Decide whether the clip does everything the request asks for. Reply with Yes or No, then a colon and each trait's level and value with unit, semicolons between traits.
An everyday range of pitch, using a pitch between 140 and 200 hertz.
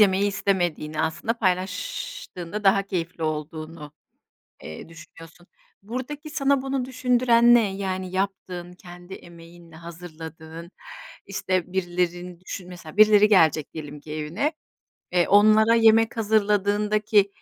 Yes: average, 4.2 semitones; medium, 185 Hz